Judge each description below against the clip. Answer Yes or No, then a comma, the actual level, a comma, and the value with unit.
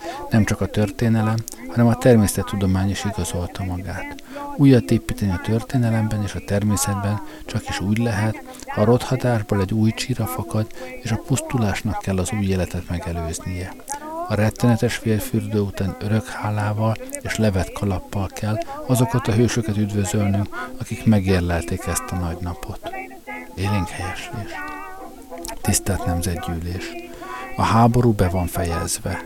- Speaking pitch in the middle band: No, low, 105 Hz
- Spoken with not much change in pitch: No, average, 3.4 semitones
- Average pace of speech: Yes, average, 135 wpm